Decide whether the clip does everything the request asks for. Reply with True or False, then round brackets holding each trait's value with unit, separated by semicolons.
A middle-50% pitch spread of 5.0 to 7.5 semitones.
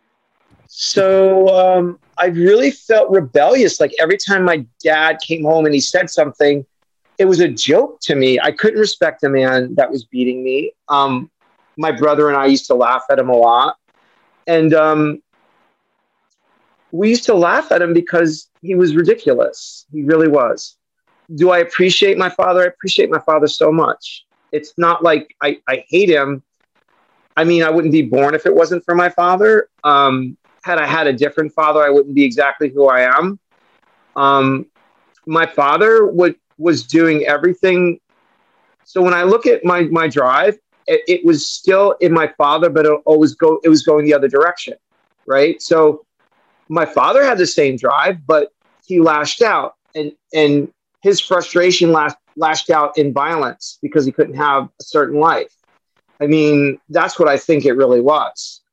False (3.7 semitones)